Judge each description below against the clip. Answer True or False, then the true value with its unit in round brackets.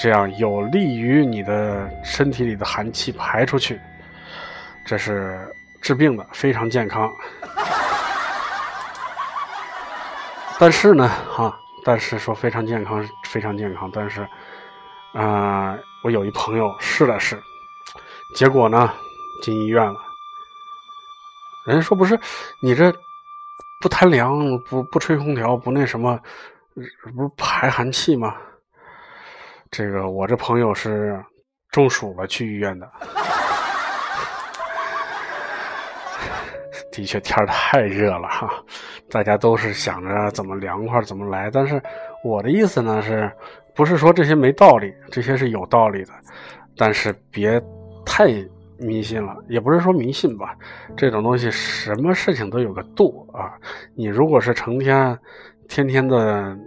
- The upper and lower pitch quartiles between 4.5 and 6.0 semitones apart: False (6.5 semitones)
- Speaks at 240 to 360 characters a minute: False (190 characters per minute)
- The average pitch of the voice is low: True (120 Hz)